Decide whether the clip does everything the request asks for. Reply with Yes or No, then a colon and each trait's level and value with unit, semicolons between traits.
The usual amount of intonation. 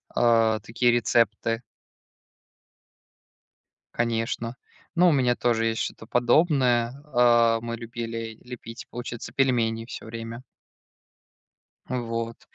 No: narrow, 1.2 semitones